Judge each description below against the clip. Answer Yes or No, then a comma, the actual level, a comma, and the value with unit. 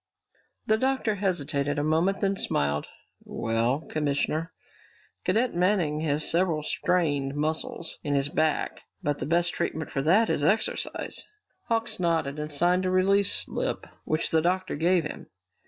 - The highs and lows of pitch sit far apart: No, average, 4.2 semitones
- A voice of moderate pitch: Yes, medium, 160 Hz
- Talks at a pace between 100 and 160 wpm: Yes, average, 150 wpm